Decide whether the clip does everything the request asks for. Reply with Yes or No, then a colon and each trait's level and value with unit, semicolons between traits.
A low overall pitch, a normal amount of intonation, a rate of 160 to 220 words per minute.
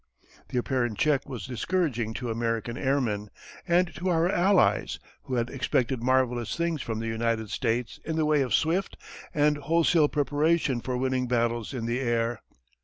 Yes: low, 130 Hz; average, 4.6 semitones; average, 165 wpm